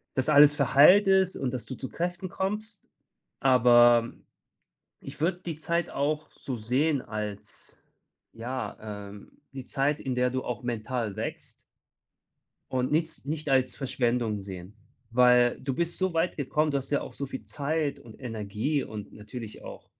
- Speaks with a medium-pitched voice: No, low, 130 Hz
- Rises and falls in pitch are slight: No, average, 4.6 semitones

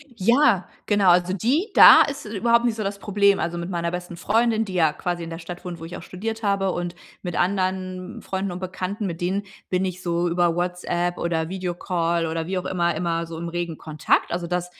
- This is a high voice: No, medium, 180 Hz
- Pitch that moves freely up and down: No, narrow, 2.4 semitones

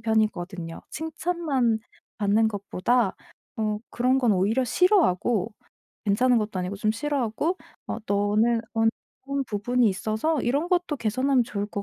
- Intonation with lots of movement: No, average, 4.5 semitones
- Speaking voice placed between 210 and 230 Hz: Yes, high, 225 Hz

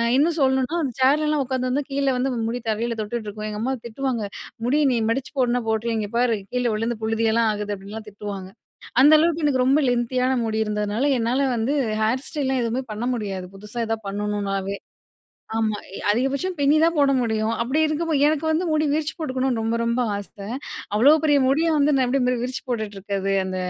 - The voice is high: Yes, high, 245 Hz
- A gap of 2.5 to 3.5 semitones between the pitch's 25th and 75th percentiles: No, average, 4.2 semitones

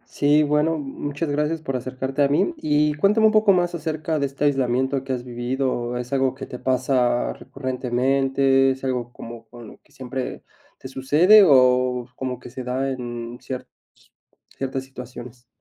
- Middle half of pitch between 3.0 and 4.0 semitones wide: No, narrow, 2.5 semitones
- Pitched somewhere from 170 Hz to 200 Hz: No, low, 130 Hz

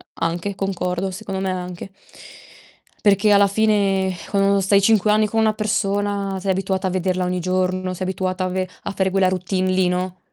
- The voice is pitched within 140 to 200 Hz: Yes, high, 190 Hz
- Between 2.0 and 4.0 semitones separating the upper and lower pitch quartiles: No, narrow, 1.4 semitones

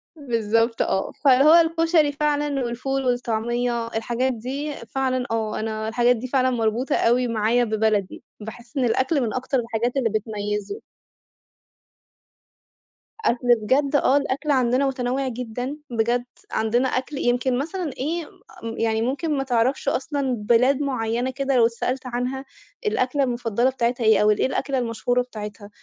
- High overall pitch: Yes, high, 245 Hz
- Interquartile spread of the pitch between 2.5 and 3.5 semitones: Yes, average, 2.9 semitones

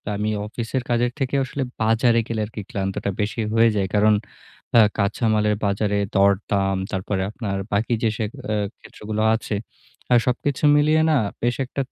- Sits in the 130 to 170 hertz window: No, low, 110 Hz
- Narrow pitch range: No, average, 3.0 semitones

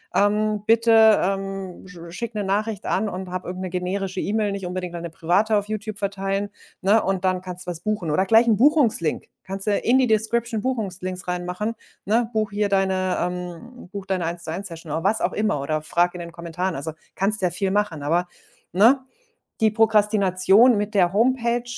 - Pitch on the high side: Yes, high, 195 Hz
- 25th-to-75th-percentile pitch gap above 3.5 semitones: No, average, 3.2 semitones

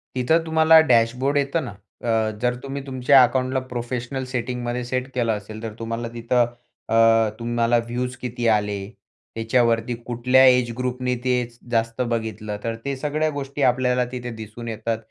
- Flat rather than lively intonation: Yes, narrow, 2.0 semitones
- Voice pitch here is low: Yes, low, 120 Hz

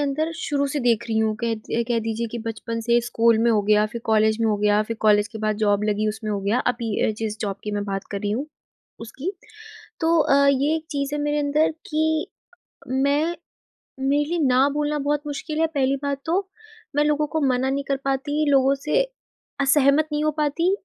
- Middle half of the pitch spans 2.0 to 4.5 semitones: No, average, 5.0 semitones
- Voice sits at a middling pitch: No, very high, 270 Hz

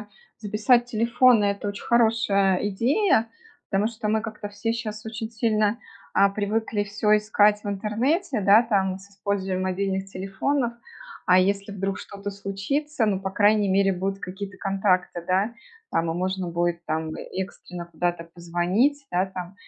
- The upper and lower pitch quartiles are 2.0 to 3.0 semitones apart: Yes, narrow, 2.6 semitones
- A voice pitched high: Yes, high, 200 Hz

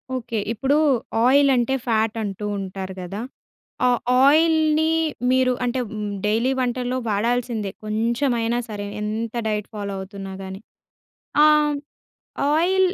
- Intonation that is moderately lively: Yes, average, 3.8 semitones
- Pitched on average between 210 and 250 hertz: Yes, high, 230 Hz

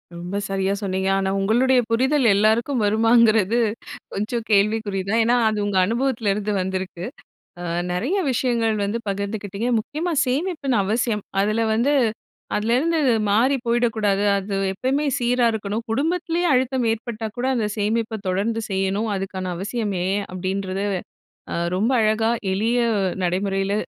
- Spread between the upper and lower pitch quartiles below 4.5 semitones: Yes, average, 3.5 semitones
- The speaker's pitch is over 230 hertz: No, high, 220 Hz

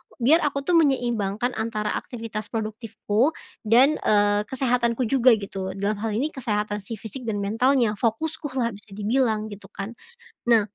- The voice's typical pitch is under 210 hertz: No, high, 225 Hz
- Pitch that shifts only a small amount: No, average, 3.5 semitones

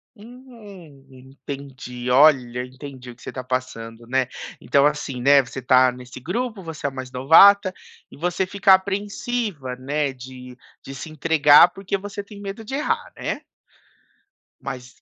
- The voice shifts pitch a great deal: Yes, wide, 7.1 semitones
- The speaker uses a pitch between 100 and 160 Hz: Yes, medium, 140 Hz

